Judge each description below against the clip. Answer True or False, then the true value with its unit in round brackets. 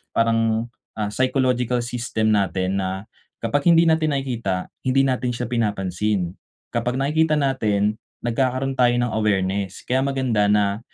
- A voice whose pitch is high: False (115 Hz)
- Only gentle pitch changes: False (4.0 semitones)